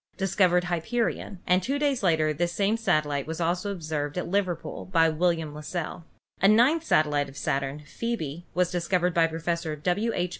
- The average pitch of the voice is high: No, medium, 175 Hz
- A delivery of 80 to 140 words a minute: No, average, 175 wpm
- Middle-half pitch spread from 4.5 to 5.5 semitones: No, average, 3.7 semitones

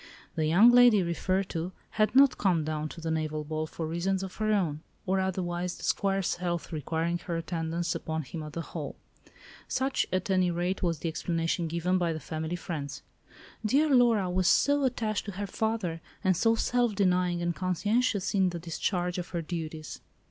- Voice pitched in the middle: Yes, medium, 180 Hz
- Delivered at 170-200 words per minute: Yes, average, 185 wpm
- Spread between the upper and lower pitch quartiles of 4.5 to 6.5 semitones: No, average, 3.2 semitones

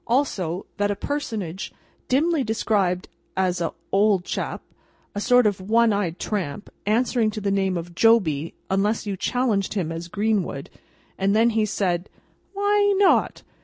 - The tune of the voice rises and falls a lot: No, average, 3.8 semitones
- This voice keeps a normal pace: Yes, average, 150 wpm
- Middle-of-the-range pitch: No, high, 205 Hz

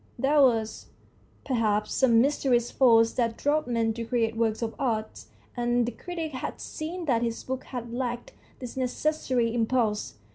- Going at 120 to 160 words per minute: Yes, average, 155 wpm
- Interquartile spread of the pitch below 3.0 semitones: Yes, narrow, 2.5 semitones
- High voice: Yes, high, 240 Hz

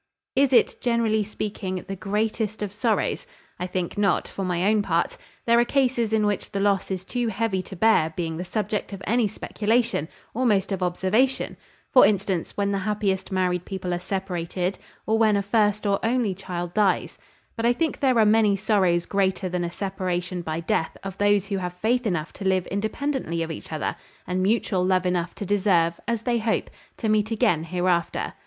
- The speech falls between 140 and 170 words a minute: No, average, 190 wpm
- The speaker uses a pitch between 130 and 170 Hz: No, high, 200 Hz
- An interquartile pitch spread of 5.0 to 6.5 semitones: No, average, 3.3 semitones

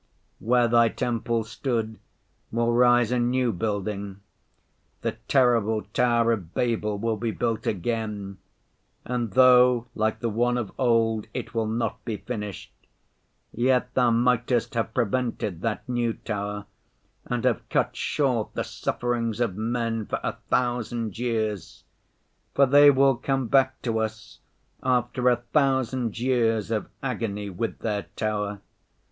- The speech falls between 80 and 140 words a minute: Yes, slow, 135 wpm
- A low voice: Yes, low, 115 Hz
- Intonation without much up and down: Yes, narrow, 2.2 semitones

